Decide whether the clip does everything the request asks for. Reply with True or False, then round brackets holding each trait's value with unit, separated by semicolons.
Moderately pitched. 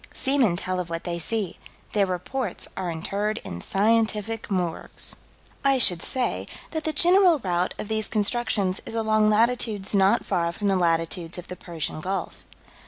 False (200 Hz)